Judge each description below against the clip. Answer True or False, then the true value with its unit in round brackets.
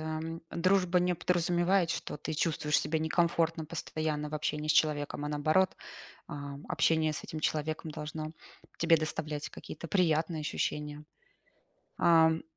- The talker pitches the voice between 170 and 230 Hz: False (155 Hz)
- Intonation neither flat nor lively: False (1.8 semitones)